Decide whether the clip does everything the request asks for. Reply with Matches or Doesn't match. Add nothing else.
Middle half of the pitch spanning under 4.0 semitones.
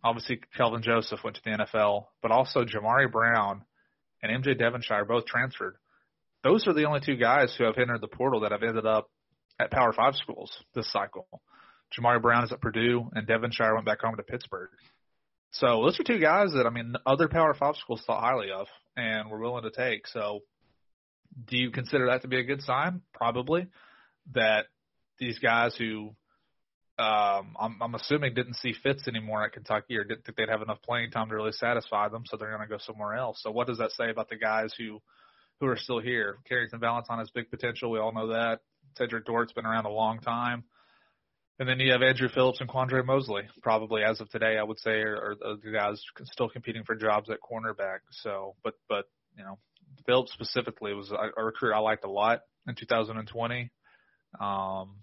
Matches